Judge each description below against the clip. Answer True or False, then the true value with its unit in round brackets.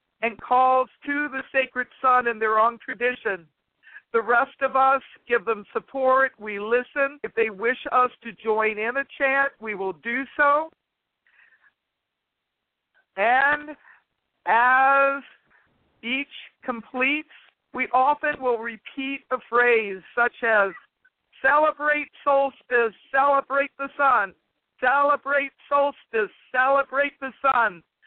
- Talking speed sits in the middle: False (115 wpm)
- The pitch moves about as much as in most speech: True (3.0 semitones)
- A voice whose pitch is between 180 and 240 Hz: False (260 Hz)